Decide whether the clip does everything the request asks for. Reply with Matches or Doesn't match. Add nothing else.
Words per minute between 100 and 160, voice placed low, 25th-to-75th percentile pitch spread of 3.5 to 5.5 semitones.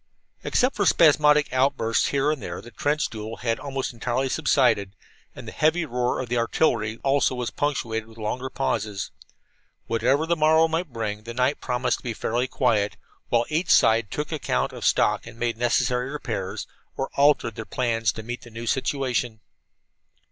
Doesn't match